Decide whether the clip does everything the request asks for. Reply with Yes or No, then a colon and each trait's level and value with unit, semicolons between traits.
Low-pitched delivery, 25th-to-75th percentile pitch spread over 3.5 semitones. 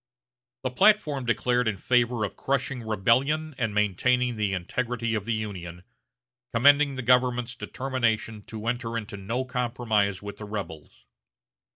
No: low, 115 Hz; average, 3.2 semitones